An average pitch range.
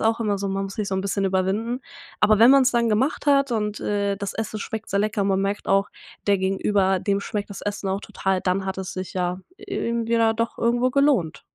Yes: average, 3.0 semitones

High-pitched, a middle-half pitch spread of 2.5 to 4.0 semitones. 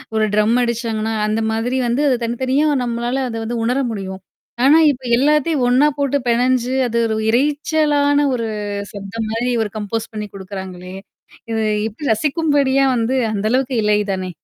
Yes: high, 235 Hz; average, 3.7 semitones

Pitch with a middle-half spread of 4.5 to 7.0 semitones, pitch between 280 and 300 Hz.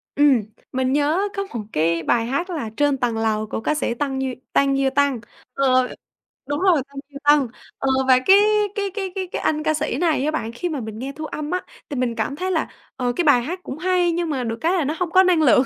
Yes: average, 4.8 semitones; very high, 285 Hz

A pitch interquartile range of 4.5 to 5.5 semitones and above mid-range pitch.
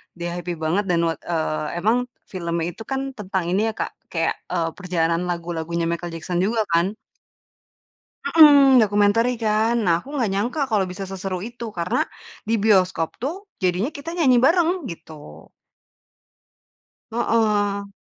Yes: average, 4.9 semitones; high, 195 Hz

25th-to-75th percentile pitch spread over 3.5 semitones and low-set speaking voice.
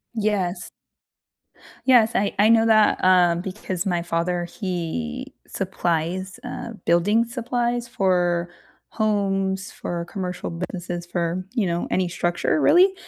No: average, 4.1 semitones; medium, 185 Hz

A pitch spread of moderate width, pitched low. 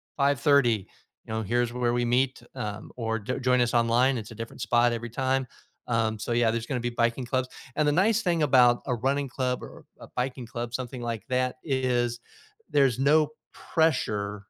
No: narrow, 2.2 semitones; low, 120 Hz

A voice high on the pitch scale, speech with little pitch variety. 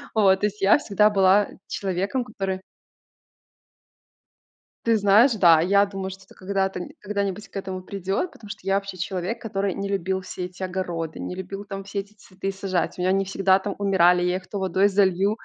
Yes: high, 195 Hz; narrow, 1.4 semitones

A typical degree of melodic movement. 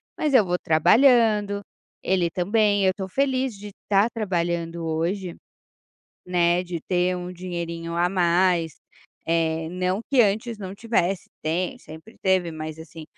Yes: average, 3.3 semitones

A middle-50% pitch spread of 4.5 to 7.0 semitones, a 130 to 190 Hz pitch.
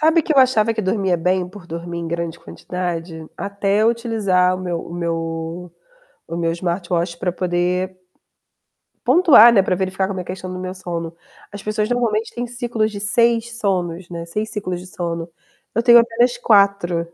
No: average, 4.1 semitones; medium, 185 Hz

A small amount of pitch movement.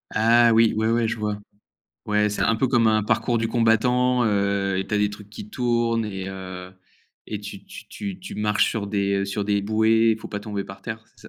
Yes: narrow, 2.3 semitones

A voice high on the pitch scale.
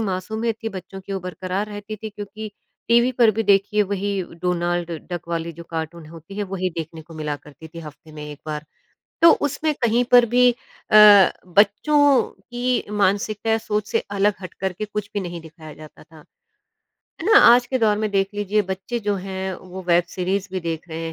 Yes: high, 195 Hz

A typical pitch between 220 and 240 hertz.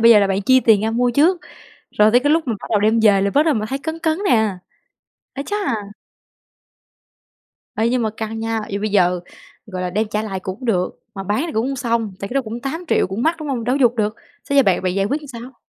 Yes: high, 225 Hz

